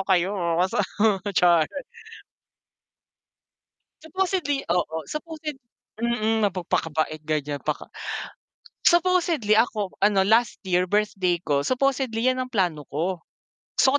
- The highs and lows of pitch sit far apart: Yes, wide, 6.8 semitones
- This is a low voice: No, high, 205 Hz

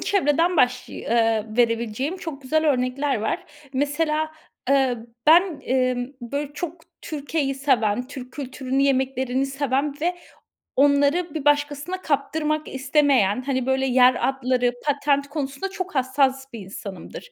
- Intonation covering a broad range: No, average, 2.9 semitones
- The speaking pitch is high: Yes, very high, 275 Hz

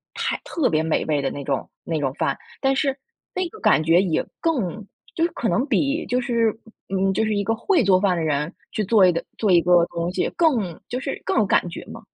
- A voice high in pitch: Yes, high, 200 Hz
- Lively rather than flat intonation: Yes, wide, 7.3 semitones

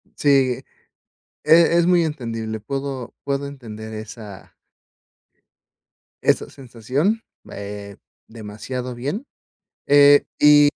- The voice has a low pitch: Yes, low, 130 Hz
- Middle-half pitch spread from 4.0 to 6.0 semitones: Yes, average, 4.7 semitones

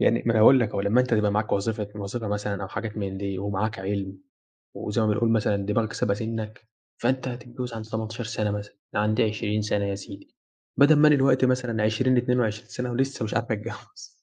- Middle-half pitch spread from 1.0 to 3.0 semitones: Yes, average, 2.7 semitones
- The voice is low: Yes, low, 110 Hz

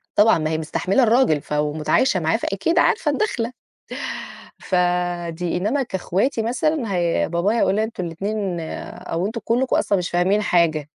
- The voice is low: No, high, 190 Hz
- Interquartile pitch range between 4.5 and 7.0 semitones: Yes, average, 5.1 semitones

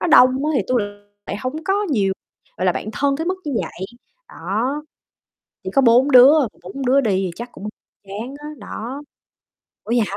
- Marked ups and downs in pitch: No, average, 5.0 semitones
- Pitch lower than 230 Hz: No, very high, 255 Hz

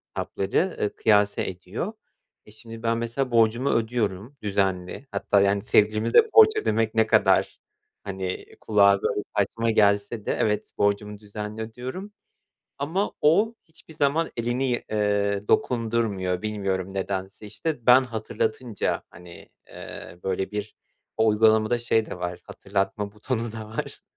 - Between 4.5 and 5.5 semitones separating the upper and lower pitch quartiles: No, average, 2.9 semitones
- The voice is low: Yes, low, 110 Hz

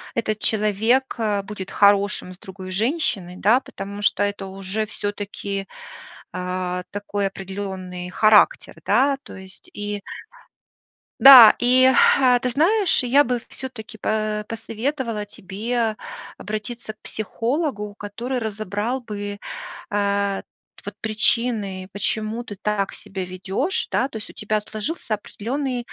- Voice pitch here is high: Yes, high, 210 Hz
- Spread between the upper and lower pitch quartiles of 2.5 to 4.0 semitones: Yes, average, 3.2 semitones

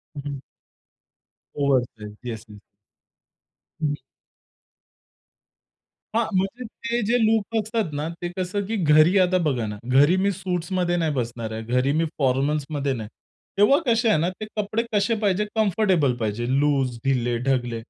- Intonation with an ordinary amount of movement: No, wide, 8.0 semitones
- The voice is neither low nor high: Yes, medium, 150 Hz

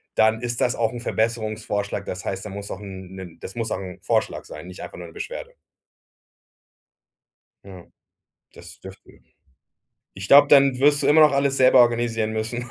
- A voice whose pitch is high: No, low, 110 Hz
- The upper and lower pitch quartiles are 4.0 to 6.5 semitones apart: Yes, average, 4.7 semitones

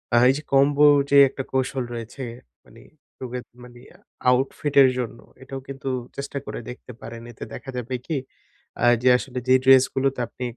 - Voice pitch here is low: Yes, low, 130 Hz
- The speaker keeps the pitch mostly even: Yes, narrow, 1.7 semitones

